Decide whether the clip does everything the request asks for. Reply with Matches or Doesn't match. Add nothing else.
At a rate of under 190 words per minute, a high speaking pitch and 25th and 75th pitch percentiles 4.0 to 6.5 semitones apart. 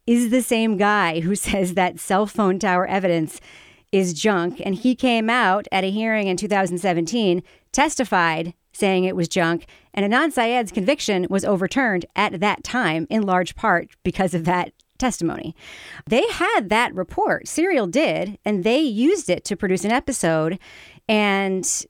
Matches